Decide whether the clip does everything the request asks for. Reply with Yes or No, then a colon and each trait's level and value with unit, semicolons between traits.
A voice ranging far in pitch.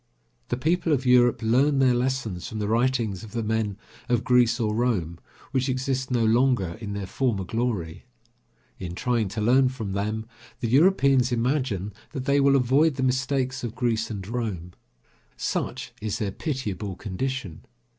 No: average, 3.7 semitones